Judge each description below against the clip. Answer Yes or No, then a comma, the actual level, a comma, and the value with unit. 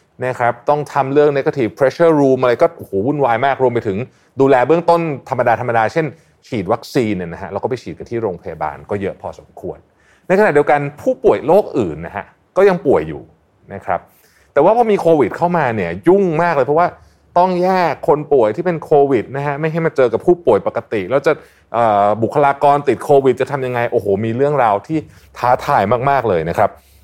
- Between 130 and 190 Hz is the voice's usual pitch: Yes, medium, 140 Hz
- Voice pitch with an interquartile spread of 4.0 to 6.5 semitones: Yes, average, 5.1 semitones